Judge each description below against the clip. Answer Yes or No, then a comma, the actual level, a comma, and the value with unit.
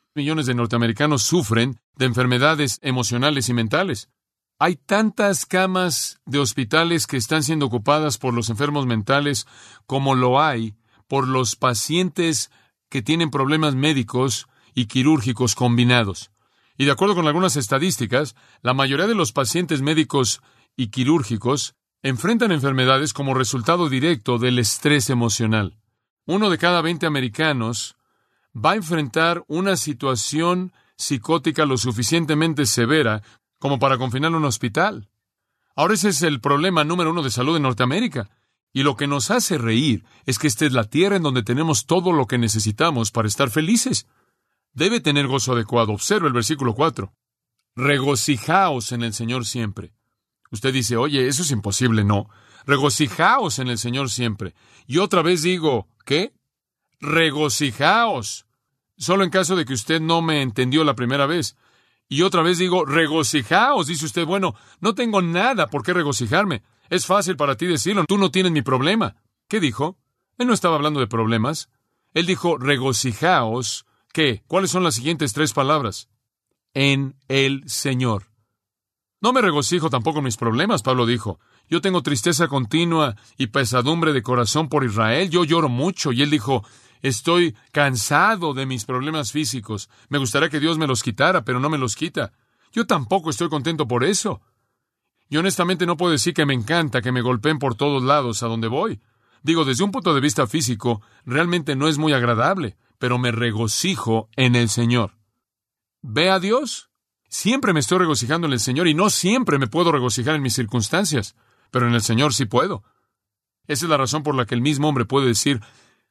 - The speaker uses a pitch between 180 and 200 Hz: No, medium, 140 Hz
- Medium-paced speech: Yes, average, 165 wpm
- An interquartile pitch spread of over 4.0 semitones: Yes, average, 5.0 semitones